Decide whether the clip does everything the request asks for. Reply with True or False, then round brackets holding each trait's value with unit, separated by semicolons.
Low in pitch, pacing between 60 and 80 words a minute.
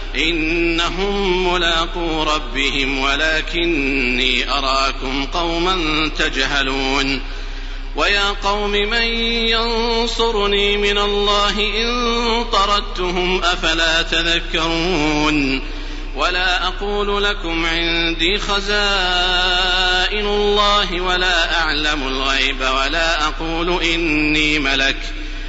False (170 Hz; 70 wpm)